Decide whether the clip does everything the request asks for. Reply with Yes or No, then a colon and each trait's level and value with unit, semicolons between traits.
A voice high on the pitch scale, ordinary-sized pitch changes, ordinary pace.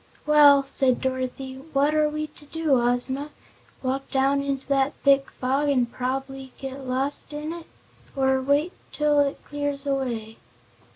No: very high, 275 Hz; narrow, 1.6 semitones; average, 150 wpm